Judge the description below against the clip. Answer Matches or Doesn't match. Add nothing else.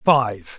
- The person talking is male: Matches